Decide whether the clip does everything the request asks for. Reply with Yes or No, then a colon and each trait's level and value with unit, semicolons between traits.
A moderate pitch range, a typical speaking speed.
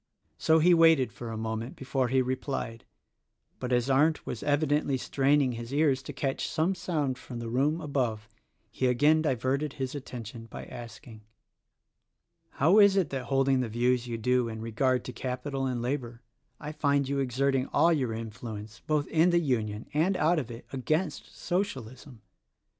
Yes: average, 3.7 semitones; average, 170 wpm